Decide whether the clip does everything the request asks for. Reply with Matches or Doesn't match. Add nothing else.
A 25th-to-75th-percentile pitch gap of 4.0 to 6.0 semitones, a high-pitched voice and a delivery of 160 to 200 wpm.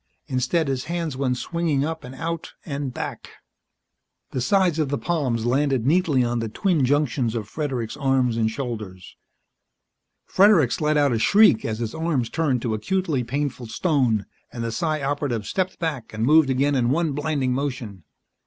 Doesn't match